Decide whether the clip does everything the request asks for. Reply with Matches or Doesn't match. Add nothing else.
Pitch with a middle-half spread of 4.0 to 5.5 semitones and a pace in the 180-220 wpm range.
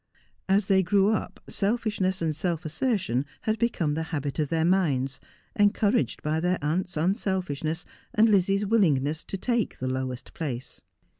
Doesn't match